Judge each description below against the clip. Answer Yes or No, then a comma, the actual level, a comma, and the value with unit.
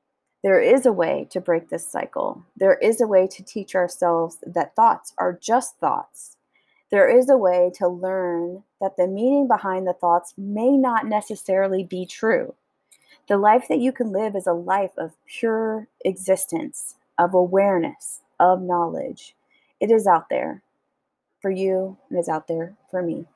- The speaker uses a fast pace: No, average, 170 wpm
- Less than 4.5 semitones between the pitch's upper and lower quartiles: Yes, average, 3.8 semitones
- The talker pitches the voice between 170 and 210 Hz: Yes, high, 190 Hz